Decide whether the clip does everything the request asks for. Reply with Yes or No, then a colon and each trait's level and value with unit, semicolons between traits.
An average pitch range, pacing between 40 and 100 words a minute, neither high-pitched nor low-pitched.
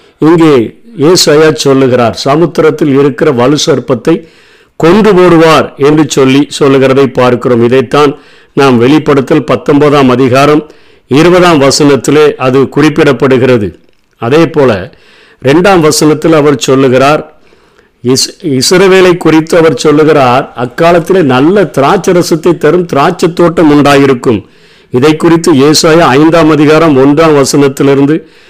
Yes: average, 3.0 semitones; average, 95 wpm; medium, 150 Hz